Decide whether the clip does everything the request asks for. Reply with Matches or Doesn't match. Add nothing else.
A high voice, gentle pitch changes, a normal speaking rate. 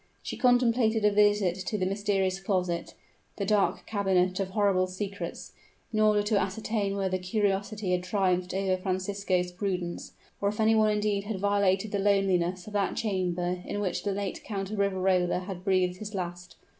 Matches